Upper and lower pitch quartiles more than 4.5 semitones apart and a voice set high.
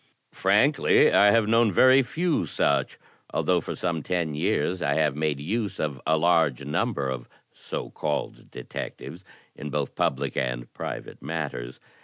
No: wide, 5.4 semitones; very low, 80 Hz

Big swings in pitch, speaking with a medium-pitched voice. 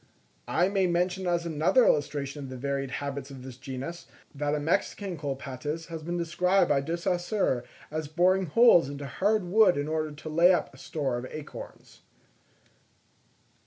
No: average, 4.1 semitones; medium, 155 Hz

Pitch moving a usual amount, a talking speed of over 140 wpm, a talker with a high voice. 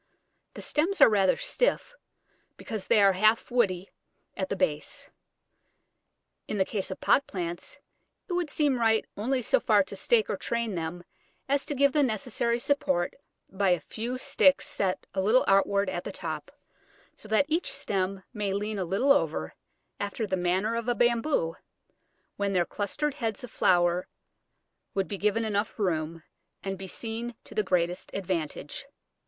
Yes: average, 4.4 semitones; average, 165 wpm; high, 205 Hz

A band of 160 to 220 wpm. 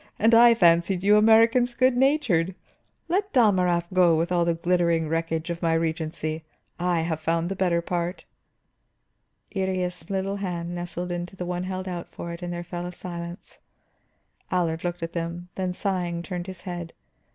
Yes: average, 170 wpm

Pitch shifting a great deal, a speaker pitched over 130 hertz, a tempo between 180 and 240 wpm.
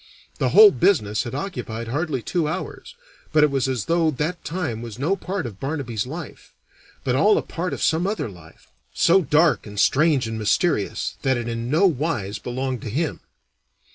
Yes: wide, 6.4 semitones; medium, 140 Hz; average, 185 wpm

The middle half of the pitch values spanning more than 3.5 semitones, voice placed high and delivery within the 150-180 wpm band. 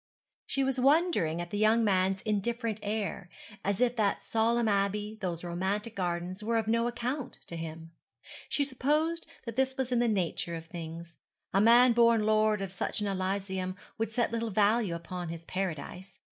Yes: average, 4.1 semitones; high, 210 Hz; average, 175 wpm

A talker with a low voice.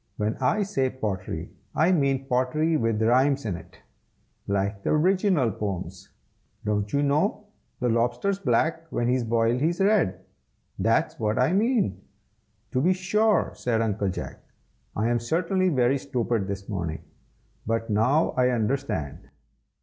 Yes: low, 125 Hz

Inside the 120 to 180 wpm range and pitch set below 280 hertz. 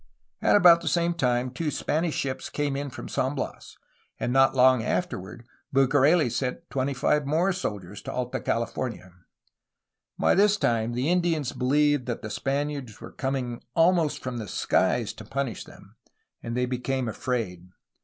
Yes: average, 160 wpm; low, 135 Hz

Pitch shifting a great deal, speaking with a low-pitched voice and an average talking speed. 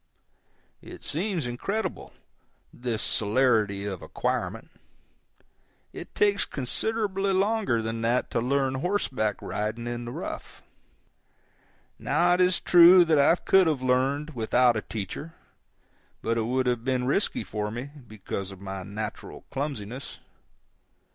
No: wide, 7.1 semitones; low, 125 Hz; slow, 130 wpm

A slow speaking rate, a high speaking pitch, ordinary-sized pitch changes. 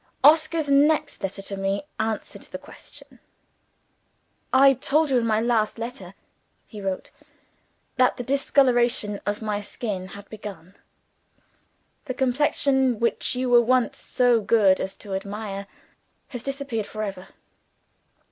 Yes: slow, 130 wpm; high, 230 Hz; average, 4.5 semitones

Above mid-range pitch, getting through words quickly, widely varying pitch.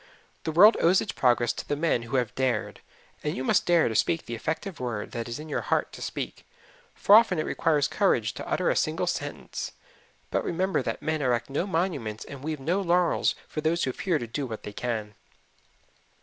No: medium, 150 Hz; fast, 210 wpm; wide, 6.0 semitones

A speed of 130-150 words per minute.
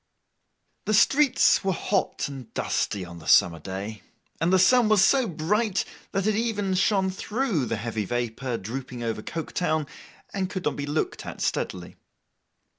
No: average, 160 wpm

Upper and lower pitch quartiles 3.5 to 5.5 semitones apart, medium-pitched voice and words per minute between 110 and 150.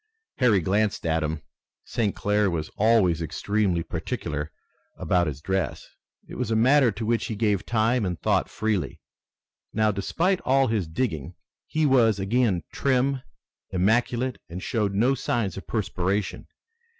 No: average, 4.7 semitones; low, 105 Hz; average, 145 wpm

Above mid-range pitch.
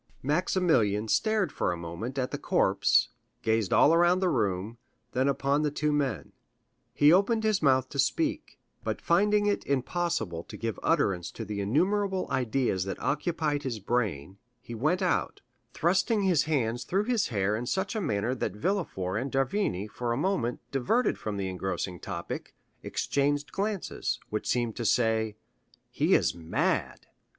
No: low, 130 Hz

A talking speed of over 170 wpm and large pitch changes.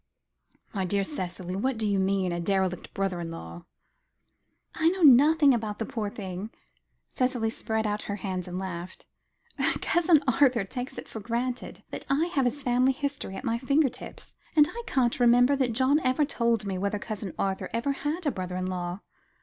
Yes: average, 185 wpm; wide, 5.7 semitones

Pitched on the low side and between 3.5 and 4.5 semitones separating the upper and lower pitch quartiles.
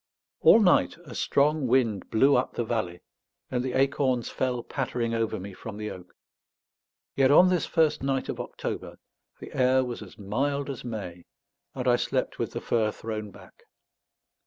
Yes: low, 125 Hz; average, 3.9 semitones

